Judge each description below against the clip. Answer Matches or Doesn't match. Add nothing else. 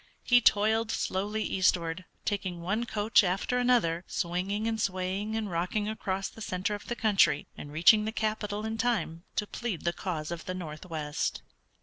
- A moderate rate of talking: Matches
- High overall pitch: Matches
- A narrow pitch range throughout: Doesn't match